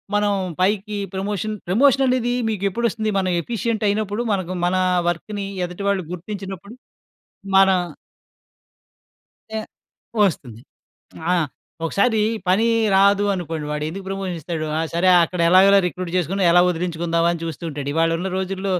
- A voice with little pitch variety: No, average, 3.1 semitones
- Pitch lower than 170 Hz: No, high, 190 Hz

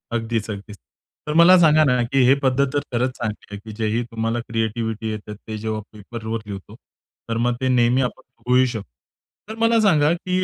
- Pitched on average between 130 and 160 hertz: No, low, 120 Hz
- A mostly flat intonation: No, average, 3.4 semitones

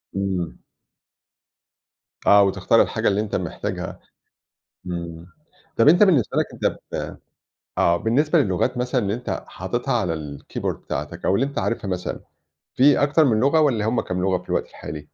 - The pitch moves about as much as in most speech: No, wide, 7.0 semitones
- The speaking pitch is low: Yes, low, 105 Hz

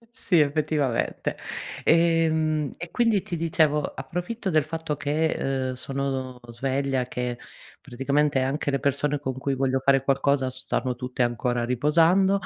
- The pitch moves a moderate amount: Yes, average, 3.4 semitones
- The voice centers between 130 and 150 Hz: Yes, medium, 140 Hz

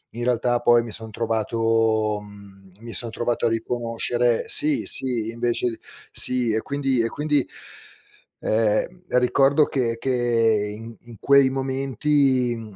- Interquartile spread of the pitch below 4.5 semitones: Yes, narrow, 2.6 semitones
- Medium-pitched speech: No, low, 120 Hz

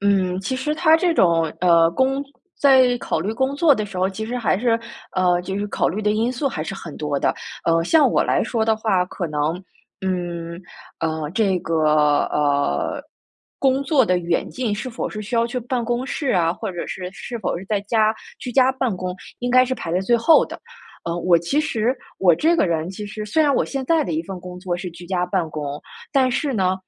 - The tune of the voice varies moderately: No, wide, 6.2 semitones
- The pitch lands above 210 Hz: No, high, 200 Hz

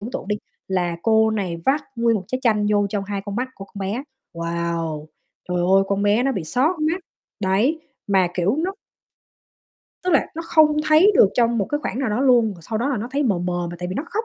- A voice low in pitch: No, high, 210 Hz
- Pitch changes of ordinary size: No, wide, 6.0 semitones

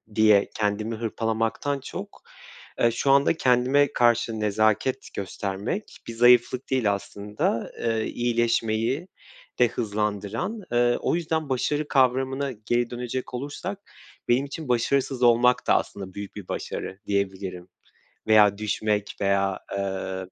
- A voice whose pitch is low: Yes, low, 115 Hz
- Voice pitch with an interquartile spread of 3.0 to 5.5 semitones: Yes, average, 3.9 semitones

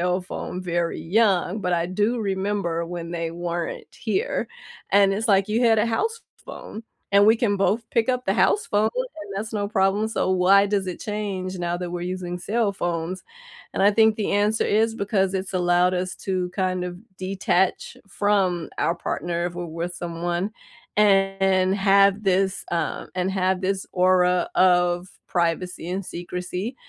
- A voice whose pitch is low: No, high, 190 Hz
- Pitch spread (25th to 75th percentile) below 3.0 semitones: Yes, narrow, 2.5 semitones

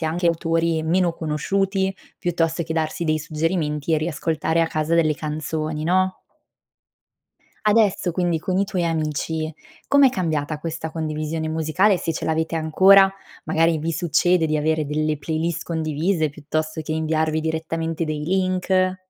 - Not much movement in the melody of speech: Yes, narrow, 2.1 semitones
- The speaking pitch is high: No, medium, 160 Hz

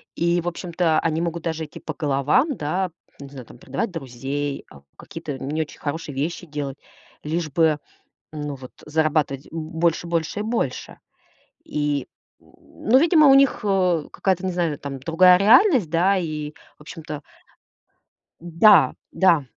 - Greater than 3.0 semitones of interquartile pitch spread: Yes, average, 3.5 semitones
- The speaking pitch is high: No, medium, 160 Hz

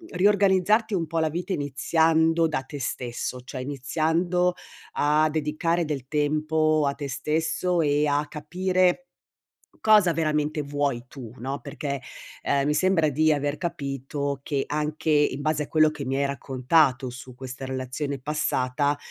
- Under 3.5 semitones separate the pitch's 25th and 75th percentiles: Yes, average, 2.7 semitones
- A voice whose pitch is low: No, medium, 150 Hz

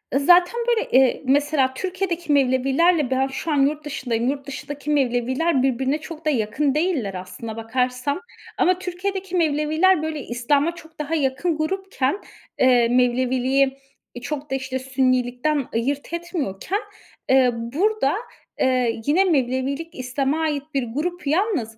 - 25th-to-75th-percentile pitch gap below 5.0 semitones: Yes, average, 4.0 semitones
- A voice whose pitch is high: Yes, very high, 280 Hz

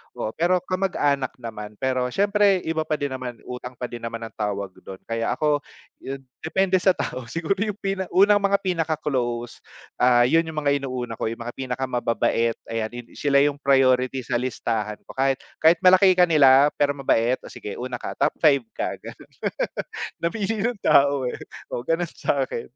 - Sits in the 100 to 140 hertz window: Yes, low, 135 Hz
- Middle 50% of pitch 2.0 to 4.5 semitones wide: No, wide, 5.6 semitones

